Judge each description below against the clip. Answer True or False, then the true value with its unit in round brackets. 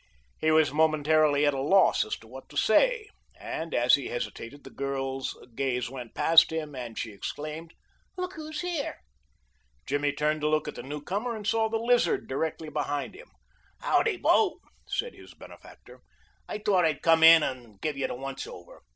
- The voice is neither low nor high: True (155 Hz)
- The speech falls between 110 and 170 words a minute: False (180 wpm)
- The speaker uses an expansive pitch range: True (6.8 semitones)